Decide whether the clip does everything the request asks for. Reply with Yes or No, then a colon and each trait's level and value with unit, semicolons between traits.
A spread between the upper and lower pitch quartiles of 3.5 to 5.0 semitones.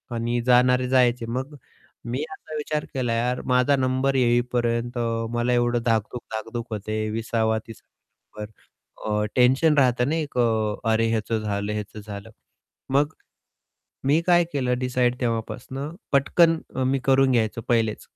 No: average, 2.7 semitones